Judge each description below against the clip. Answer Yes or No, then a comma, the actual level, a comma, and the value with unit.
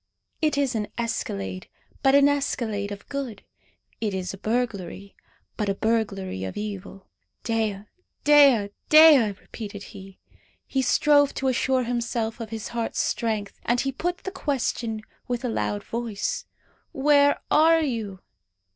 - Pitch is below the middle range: No, high, 230 Hz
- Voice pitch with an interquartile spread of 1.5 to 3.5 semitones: No, average, 5.0 semitones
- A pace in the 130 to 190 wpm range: Yes, average, 140 wpm